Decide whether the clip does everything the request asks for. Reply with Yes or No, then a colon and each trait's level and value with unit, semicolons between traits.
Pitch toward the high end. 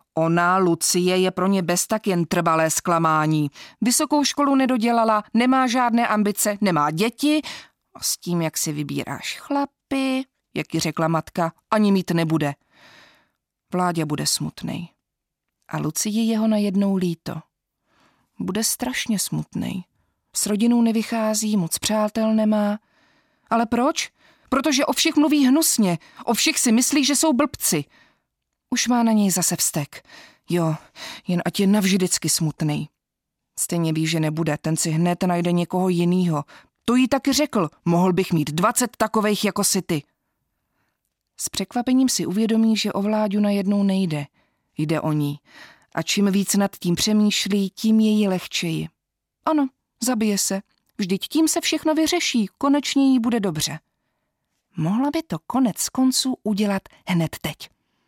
Yes: high, 205 Hz